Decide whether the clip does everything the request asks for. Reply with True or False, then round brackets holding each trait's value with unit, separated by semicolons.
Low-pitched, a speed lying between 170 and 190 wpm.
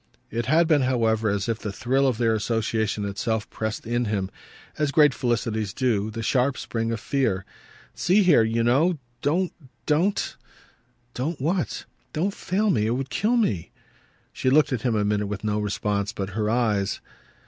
True (115 Hz; 180 wpm)